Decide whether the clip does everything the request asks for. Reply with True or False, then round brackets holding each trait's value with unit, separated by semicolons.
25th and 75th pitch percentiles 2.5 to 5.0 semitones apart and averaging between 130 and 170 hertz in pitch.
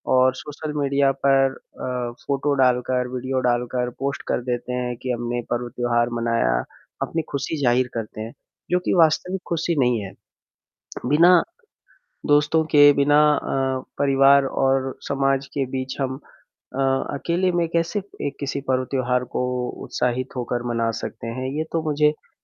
True (2.8 semitones; 135 Hz)